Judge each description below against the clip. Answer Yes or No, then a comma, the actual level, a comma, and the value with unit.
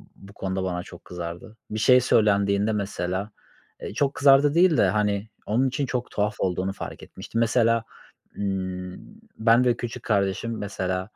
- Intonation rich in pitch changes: No, average, 3.6 semitones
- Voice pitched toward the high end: No, low, 105 Hz